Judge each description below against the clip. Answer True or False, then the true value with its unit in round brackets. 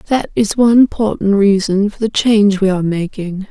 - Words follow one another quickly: False (190 wpm)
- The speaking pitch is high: True (205 Hz)